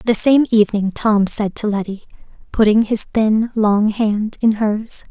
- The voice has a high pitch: Yes, high, 215 Hz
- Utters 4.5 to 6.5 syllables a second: No, 4.2 syllables/s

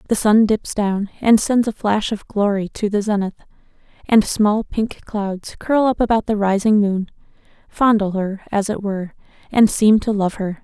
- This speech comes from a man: No, female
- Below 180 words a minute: No, average, 185 wpm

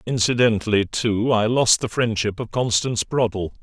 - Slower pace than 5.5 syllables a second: Yes, 5.0 syllables/s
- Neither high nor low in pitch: No, low, 110 Hz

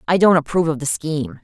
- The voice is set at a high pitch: No, medium, 160 Hz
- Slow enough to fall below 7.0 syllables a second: No, 7.1 syllables/s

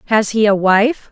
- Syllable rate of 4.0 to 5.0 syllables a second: Yes, 4.5 syllables/s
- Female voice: Yes, female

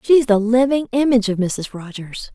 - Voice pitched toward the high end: Yes, high, 230 Hz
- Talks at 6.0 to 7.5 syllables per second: No, 5.0 syllables/s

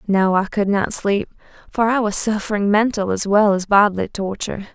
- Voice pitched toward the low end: No, high, 205 Hz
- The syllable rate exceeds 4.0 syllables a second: Yes, 5.4 syllables/s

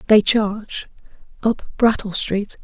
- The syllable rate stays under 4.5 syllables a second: Yes, 3.9 syllables/s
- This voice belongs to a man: No, female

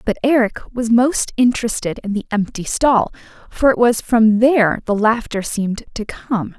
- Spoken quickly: No, average, 175 wpm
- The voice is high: Yes, high, 230 Hz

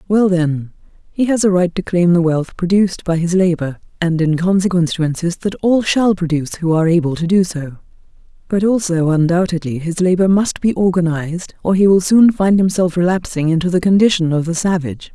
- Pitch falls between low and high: Yes, medium, 175 Hz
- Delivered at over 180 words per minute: Yes, average, 200 wpm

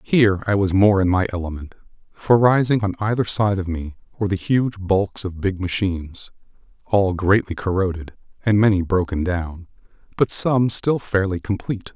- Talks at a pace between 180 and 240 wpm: No, average, 165 wpm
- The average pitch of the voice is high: No, low, 100 Hz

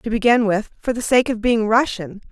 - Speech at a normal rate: No, fast, 235 wpm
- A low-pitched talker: No, high, 225 Hz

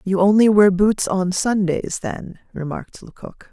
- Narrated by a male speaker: No, female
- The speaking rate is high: No, average, 155 wpm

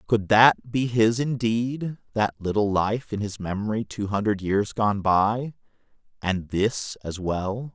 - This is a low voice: Yes, low, 105 Hz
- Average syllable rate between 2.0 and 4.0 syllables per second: Yes, 3.8 syllables/s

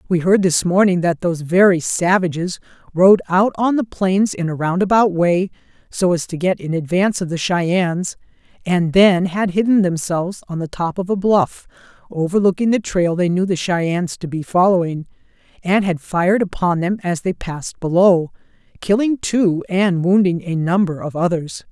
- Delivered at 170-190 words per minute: Yes, average, 175 wpm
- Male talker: No, female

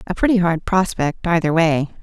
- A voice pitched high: No, medium, 170 Hz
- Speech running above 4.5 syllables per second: Yes, 5.0 syllables/s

